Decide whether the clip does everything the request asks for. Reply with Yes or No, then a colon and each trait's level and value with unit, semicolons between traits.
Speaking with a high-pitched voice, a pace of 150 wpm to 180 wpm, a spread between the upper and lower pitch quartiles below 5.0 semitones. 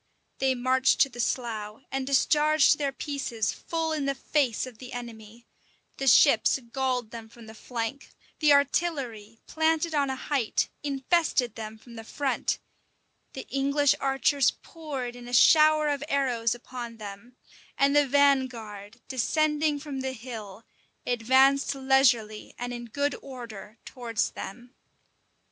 No: very high, 260 Hz; average, 140 wpm; average, 3.4 semitones